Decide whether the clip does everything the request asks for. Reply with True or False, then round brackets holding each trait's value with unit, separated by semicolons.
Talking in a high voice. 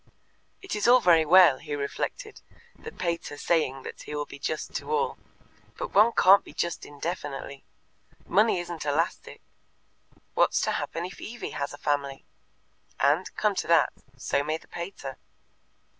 False (165 Hz)